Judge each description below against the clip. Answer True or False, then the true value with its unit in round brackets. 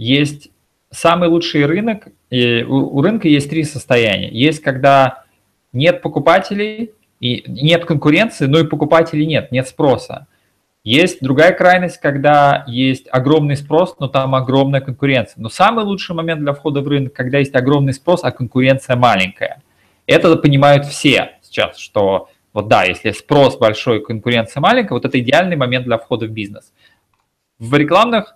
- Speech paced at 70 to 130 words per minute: False (150 wpm)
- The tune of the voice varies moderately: True (4.3 semitones)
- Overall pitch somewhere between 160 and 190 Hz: False (140 Hz)